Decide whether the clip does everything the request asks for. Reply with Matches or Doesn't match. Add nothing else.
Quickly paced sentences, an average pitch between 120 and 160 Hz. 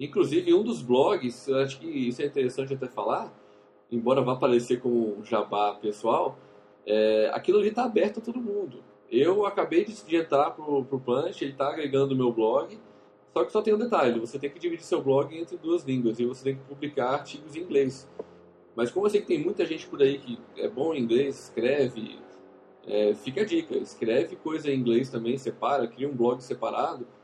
Matches